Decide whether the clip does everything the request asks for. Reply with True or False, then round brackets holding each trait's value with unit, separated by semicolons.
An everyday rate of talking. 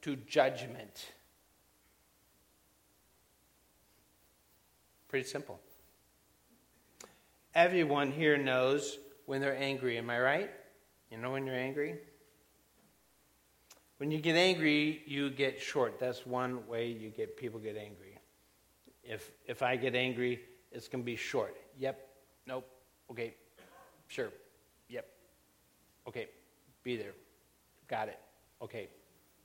False (110 wpm)